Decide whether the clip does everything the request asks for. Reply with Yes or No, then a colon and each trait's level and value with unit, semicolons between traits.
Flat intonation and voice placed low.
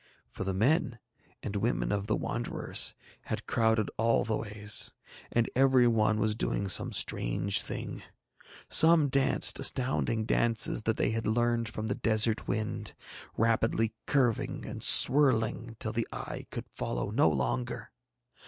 Yes: narrow, 1.8 semitones; low, 115 Hz